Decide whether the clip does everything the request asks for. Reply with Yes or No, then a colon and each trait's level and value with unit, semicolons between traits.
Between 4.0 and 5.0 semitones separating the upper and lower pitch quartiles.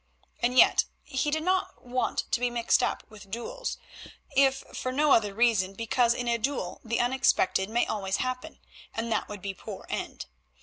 No: average, 3.5 semitones